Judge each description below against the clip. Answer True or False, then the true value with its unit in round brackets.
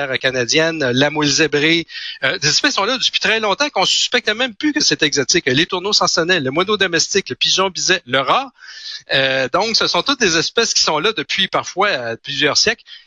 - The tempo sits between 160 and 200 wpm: False (210 wpm)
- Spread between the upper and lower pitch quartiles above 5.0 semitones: True (5.6 semitones)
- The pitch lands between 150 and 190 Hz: True (165 Hz)